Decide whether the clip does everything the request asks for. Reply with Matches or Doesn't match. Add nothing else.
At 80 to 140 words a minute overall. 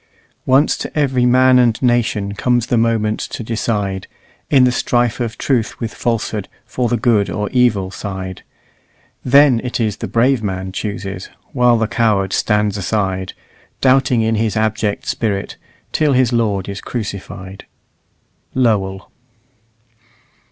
Matches